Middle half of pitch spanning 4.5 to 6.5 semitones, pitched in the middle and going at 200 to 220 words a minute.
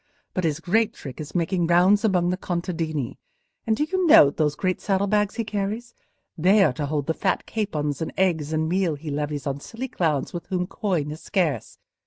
Yes: average, 4.9 semitones; medium, 175 Hz; fast, 205 wpm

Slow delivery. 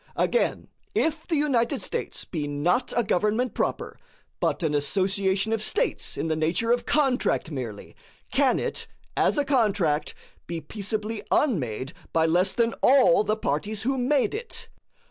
No: average, 150 wpm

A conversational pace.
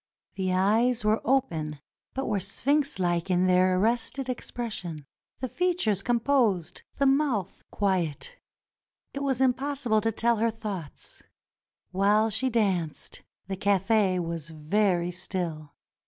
No: slow, 125 wpm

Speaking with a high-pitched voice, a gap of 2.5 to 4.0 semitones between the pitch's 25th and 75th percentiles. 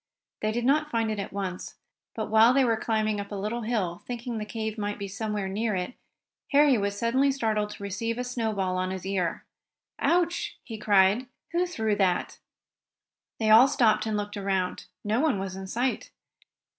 Yes: high, 215 Hz; average, 3.0 semitones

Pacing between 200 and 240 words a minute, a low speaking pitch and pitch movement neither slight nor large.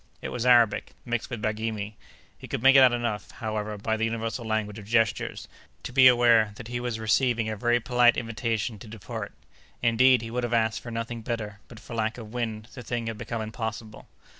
No: fast, 205 wpm; low, 115 Hz; narrow, 1.7 semitones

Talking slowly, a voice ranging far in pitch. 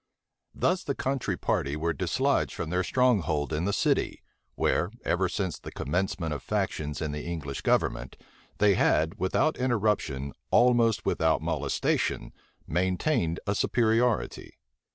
Yes: slow, 130 wpm; wide, 6.5 semitones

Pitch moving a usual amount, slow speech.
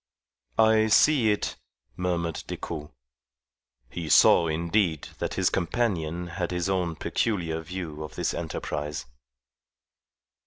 Yes: average, 3.4 semitones; slow, 110 wpm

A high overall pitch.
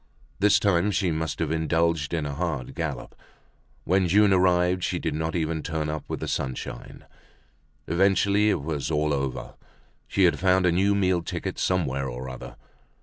No: very low, 85 Hz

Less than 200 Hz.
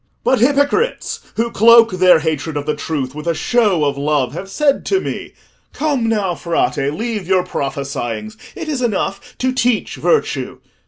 Yes: high, 190 Hz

